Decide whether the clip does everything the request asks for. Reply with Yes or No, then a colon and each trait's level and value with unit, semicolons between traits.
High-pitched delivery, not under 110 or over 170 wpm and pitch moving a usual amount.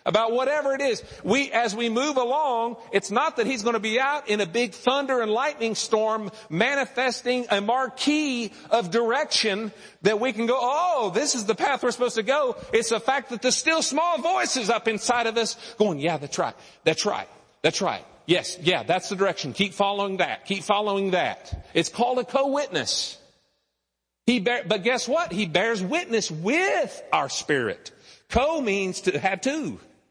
No: high, 235 Hz; average, 185 wpm; average, 4.1 semitones